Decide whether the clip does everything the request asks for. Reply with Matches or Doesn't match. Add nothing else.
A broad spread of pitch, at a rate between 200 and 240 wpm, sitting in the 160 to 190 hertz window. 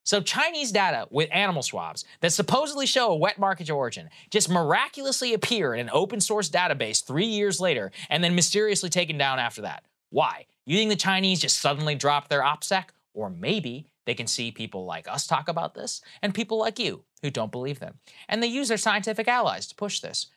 Matches